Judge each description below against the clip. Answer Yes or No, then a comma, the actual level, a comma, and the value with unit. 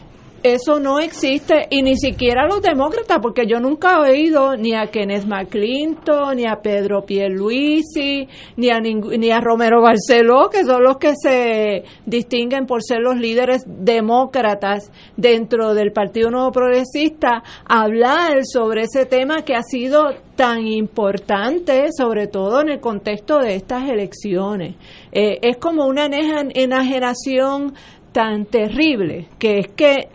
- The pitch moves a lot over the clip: No, average, 3.9 semitones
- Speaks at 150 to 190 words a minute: No, average, 140 wpm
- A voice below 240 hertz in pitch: No, high, 245 Hz